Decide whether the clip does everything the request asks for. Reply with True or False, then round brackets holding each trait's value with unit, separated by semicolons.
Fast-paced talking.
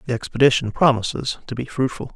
False (165 wpm)